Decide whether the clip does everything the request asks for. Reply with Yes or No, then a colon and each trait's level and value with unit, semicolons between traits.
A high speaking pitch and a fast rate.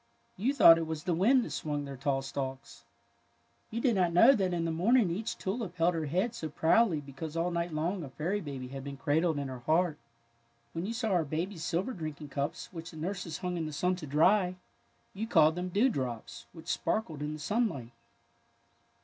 No: medium, 165 Hz; fast, 210 wpm